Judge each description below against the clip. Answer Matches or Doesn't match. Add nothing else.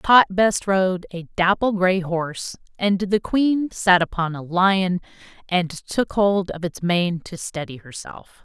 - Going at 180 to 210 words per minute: Doesn't match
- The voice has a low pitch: Doesn't match